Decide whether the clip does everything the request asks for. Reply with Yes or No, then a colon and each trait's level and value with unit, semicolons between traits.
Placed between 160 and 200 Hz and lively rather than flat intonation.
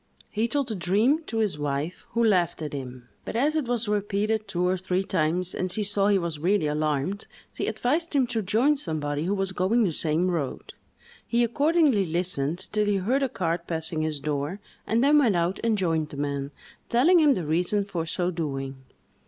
Yes: medium, 185 Hz; wide, 6.0 semitones